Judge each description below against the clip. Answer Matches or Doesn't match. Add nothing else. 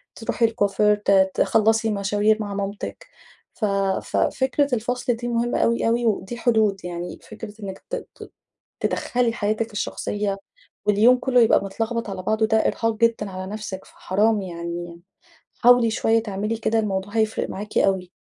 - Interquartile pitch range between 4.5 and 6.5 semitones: Doesn't match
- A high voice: Matches